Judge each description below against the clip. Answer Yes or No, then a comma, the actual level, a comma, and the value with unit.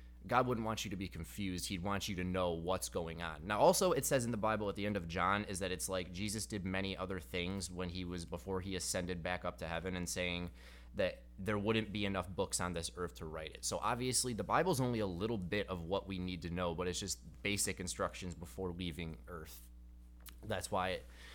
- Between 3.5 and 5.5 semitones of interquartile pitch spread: No, average, 2.7 semitones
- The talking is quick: Yes, fast, 240 wpm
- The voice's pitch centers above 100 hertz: No, very low, 90 Hz